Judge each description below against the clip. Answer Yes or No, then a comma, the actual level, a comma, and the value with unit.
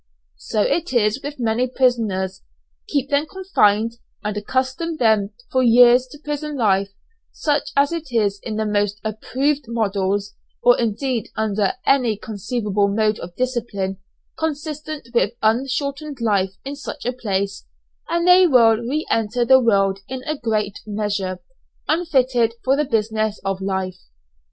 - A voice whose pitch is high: Yes, high, 230 Hz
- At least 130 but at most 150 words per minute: Yes, average, 145 wpm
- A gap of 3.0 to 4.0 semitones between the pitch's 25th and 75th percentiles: No, average, 4.8 semitones